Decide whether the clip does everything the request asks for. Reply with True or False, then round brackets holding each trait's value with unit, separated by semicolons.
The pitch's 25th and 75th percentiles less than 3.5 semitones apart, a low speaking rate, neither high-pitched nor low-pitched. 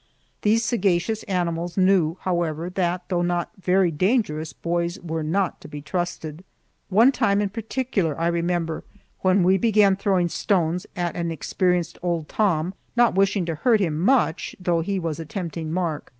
False (2.9 semitones; 165 wpm; 175 Hz)